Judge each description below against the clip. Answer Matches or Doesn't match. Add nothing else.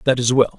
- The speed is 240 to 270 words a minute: Doesn't match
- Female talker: Doesn't match